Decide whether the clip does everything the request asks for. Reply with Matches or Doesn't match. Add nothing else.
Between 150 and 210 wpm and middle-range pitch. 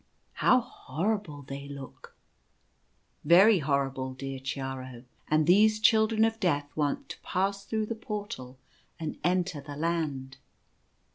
Doesn't match